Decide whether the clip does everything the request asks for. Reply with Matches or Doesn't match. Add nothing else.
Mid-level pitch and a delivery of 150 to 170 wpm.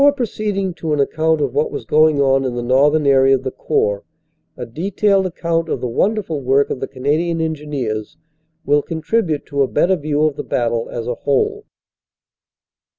Doesn't match